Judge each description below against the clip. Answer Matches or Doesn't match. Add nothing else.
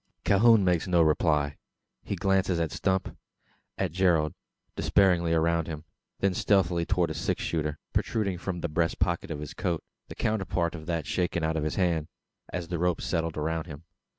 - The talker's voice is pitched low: Matches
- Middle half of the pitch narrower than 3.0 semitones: Matches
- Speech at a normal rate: Matches